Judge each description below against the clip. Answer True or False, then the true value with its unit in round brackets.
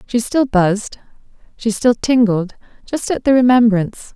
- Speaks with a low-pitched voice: False (230 Hz)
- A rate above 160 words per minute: False (145 wpm)